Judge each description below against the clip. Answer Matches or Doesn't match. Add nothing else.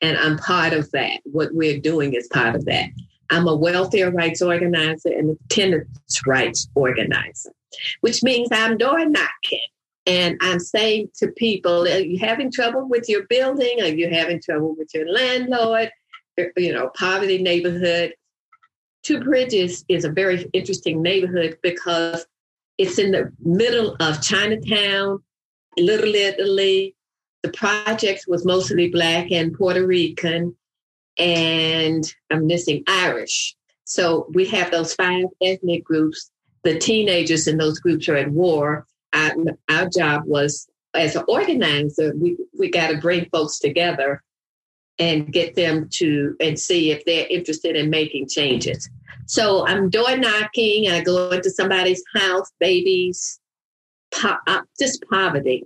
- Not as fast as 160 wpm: Matches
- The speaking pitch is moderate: Matches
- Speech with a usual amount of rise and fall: Matches